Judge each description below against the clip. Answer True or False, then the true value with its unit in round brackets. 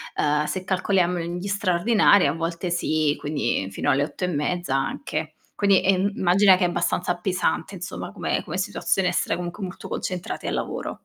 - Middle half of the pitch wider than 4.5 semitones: False (2.7 semitones)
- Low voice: False (180 Hz)